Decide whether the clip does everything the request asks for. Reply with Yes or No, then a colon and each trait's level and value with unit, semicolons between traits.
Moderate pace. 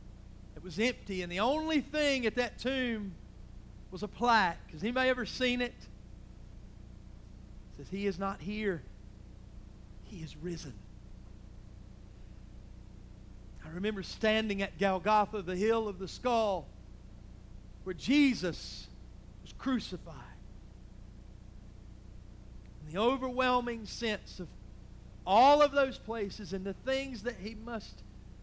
No: slow, 120 wpm